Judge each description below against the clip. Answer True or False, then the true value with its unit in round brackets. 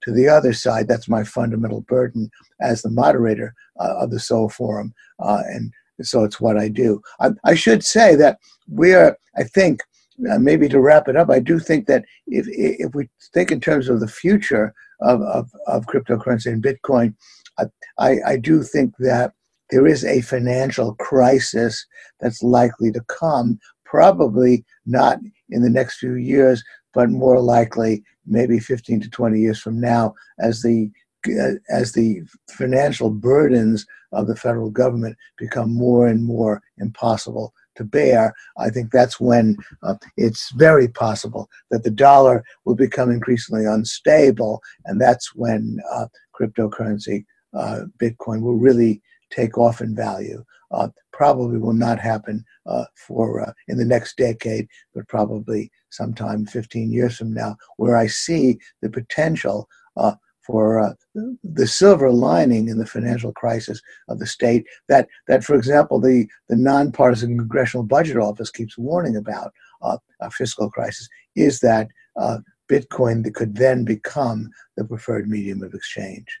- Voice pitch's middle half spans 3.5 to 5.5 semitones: False (2.5 semitones)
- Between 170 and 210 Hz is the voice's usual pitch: False (120 Hz)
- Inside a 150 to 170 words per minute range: True (160 wpm)